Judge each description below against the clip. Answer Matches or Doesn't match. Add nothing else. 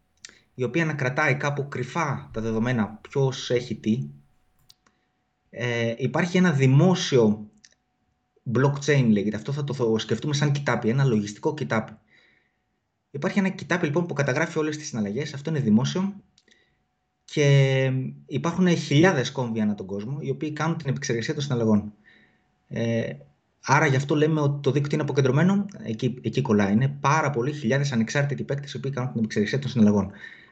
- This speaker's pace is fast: Doesn't match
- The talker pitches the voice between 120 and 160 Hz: Matches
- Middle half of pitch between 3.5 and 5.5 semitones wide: Matches